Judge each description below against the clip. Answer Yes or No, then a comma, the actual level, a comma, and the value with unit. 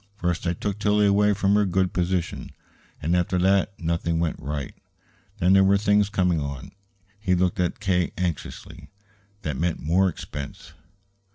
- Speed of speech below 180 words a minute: Yes, average, 160 wpm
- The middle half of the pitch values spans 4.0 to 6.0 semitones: No, average, 2.8 semitones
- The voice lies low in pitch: Yes, very low, 90 Hz